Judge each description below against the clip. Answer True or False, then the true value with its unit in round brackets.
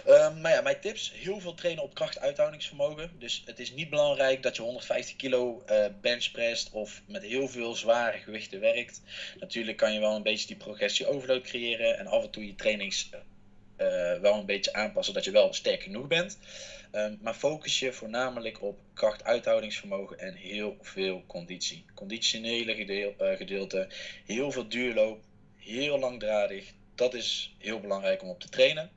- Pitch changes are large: True (8.4 semitones)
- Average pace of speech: True (170 wpm)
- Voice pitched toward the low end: True (120 Hz)